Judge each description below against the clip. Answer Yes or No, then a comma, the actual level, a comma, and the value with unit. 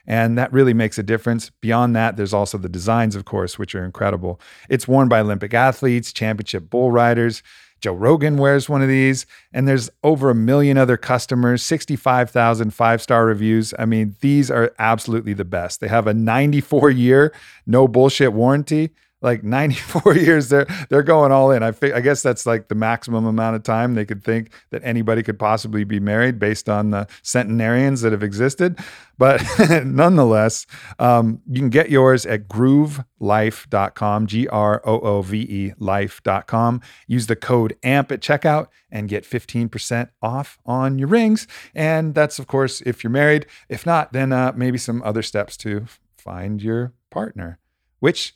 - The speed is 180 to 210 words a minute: No, average, 170 wpm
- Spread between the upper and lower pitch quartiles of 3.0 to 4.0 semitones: Yes, average, 3.7 semitones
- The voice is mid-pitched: No, low, 120 Hz